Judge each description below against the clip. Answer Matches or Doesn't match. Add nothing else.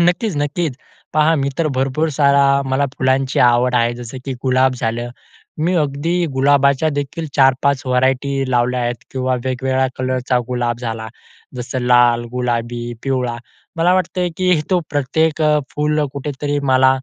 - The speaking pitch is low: Matches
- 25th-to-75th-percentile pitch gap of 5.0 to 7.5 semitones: Doesn't match